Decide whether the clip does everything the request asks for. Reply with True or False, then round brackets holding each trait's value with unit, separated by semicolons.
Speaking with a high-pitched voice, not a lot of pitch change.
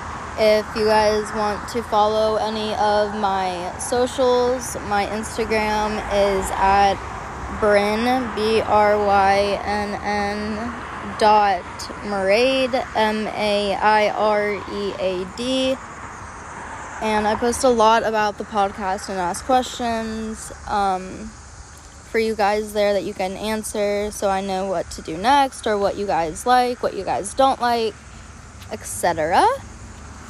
True (210 Hz; 2.1 semitones)